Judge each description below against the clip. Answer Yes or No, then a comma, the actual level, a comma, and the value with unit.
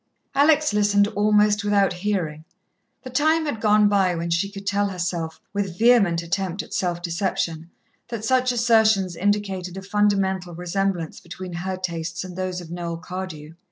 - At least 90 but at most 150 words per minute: No, average, 160 wpm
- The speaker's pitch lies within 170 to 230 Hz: Yes, high, 190 Hz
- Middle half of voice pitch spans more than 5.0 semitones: No, average, 3.1 semitones